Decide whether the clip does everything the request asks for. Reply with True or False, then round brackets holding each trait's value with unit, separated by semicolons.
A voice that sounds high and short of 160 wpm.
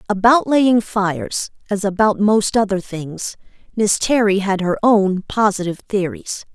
True (205 Hz; 140 wpm)